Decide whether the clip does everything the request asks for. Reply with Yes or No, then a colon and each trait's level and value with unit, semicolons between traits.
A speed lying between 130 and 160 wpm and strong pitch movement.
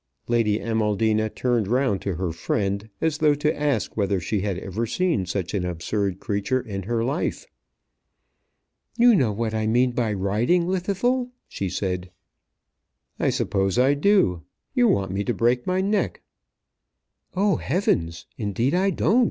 Yes: average, 150 wpm; wide, 7.4 semitones